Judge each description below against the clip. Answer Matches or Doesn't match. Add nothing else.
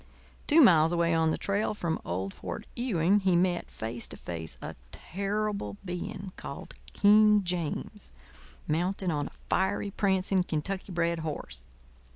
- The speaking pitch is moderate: Matches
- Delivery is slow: Doesn't match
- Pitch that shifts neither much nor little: Matches